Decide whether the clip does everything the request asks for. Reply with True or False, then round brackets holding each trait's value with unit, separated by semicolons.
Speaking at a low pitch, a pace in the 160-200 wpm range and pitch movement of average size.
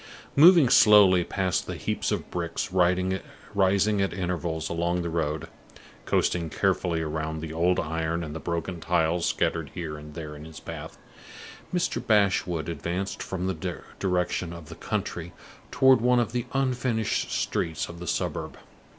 False (90 Hz; 150 wpm; 3.2 semitones)